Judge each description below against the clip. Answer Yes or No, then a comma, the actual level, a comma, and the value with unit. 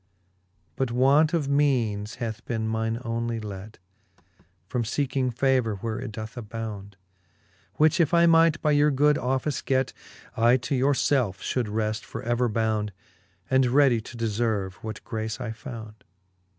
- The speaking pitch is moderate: No, low, 115 Hz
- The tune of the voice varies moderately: Yes, average, 3.5 semitones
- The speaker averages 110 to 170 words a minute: Yes, average, 155 wpm